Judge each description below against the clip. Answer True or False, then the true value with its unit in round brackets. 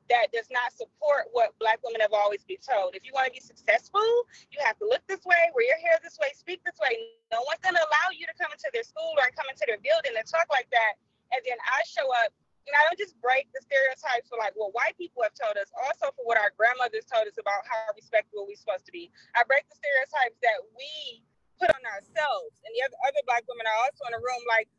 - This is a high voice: True (275 Hz)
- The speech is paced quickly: True (260 wpm)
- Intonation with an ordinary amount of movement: False (5.9 semitones)